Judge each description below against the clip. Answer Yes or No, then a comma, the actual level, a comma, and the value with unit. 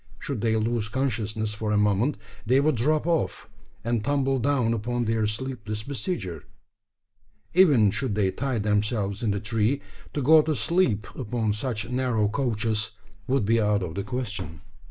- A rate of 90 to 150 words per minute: No, average, 160 wpm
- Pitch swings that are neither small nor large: Yes, average, 3.8 semitones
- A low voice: Yes, low, 115 Hz